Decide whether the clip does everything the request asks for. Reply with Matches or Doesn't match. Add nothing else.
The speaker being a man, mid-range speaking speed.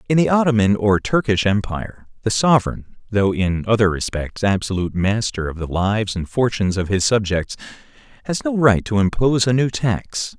Matches